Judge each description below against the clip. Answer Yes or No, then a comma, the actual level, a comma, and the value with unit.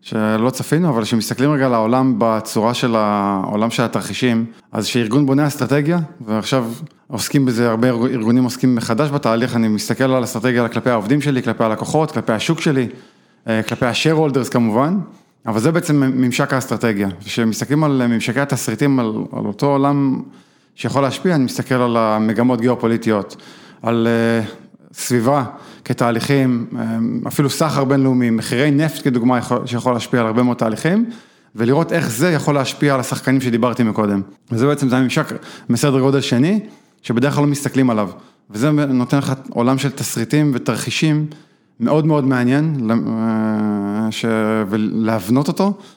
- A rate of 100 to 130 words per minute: No, average, 145 wpm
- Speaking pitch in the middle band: No, low, 125 Hz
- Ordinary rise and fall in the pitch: Yes, average, 3.7 semitones